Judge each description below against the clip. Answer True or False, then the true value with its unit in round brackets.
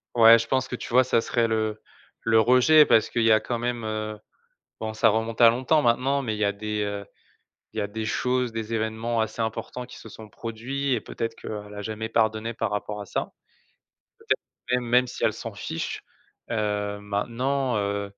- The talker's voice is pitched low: True (115 Hz)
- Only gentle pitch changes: True (2.1 semitones)